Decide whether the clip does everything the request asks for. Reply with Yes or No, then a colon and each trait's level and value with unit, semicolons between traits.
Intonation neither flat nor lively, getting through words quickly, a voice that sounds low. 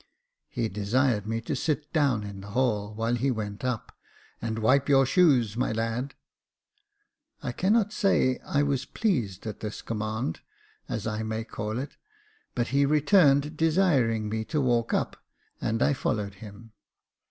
No: average, 4.5 semitones; average, 165 wpm; low, 120 Hz